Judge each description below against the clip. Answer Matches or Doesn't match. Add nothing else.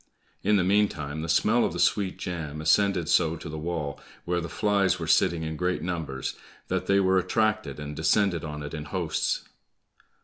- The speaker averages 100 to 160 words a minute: Doesn't match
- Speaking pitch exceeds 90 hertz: Doesn't match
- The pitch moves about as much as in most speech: Matches